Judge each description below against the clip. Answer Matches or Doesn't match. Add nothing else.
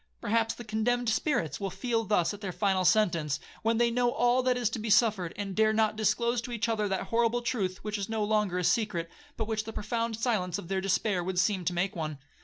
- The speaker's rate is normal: Doesn't match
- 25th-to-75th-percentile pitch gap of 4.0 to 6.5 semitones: Doesn't match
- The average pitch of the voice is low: Doesn't match